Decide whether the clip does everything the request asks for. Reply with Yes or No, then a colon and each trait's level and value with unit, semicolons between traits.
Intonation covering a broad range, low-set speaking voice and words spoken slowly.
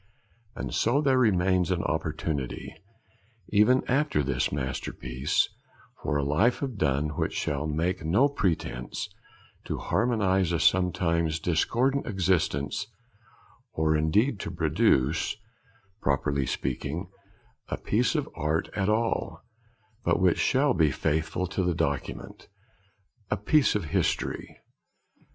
Yes: wide, 5.9 semitones; very low, 90 Hz; slow, 120 wpm